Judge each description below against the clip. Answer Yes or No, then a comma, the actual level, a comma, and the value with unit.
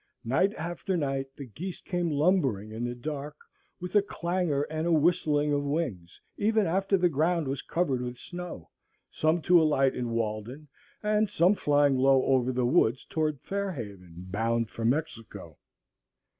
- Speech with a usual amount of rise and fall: No, wide, 5.9 semitones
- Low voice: No, medium, 145 Hz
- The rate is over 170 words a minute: No, average, 165 wpm